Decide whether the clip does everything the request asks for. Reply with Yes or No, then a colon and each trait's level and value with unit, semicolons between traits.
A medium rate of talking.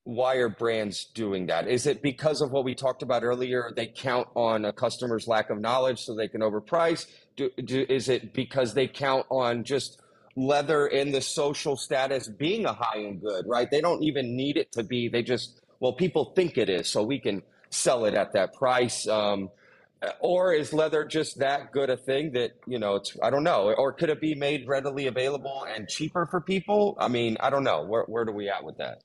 No: fast, 220 wpm